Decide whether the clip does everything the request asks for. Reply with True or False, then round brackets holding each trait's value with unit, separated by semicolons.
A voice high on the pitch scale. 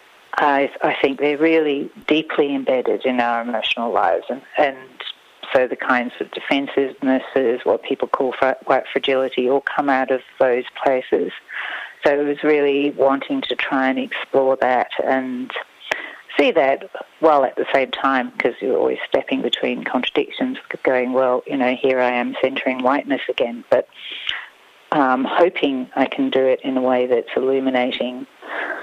False (135 Hz)